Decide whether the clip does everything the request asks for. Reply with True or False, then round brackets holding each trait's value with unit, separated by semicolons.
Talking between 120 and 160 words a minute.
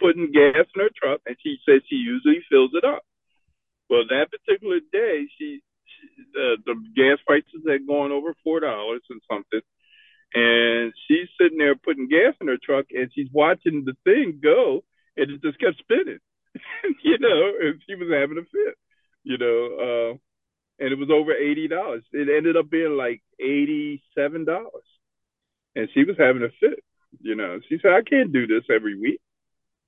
False (185 wpm)